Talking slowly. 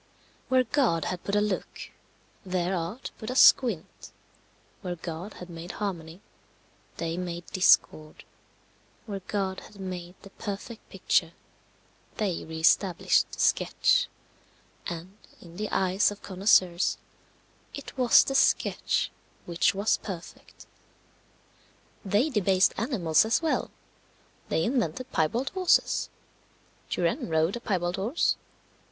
Yes: slow, 120 wpm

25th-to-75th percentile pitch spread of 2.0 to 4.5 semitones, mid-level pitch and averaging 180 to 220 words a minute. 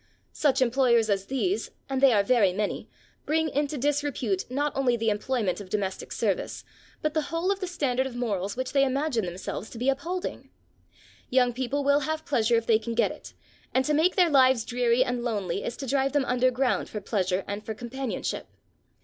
No: average, 4.1 semitones; very high, 255 Hz; average, 195 wpm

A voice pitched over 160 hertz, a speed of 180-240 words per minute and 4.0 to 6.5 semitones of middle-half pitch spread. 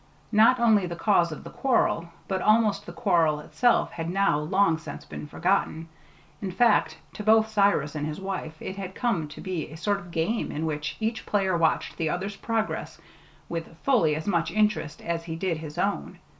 Yes: medium, 185 Hz; average, 195 wpm; average, 4.6 semitones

